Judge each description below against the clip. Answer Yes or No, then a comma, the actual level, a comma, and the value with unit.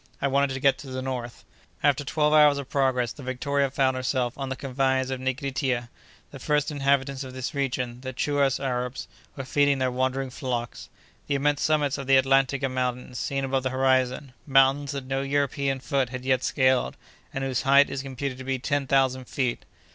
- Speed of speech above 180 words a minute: Yes, average, 190 wpm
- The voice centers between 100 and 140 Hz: Yes, low, 135 Hz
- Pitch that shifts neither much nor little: No, narrow, 1.2 semitones